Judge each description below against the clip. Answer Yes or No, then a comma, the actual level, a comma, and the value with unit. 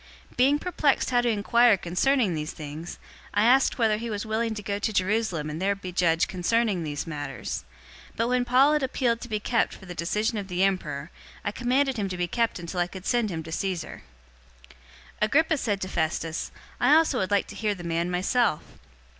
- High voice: Yes, high, 205 Hz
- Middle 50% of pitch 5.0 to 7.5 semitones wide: Yes, average, 5.3 semitones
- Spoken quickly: Yes, fast, 215 wpm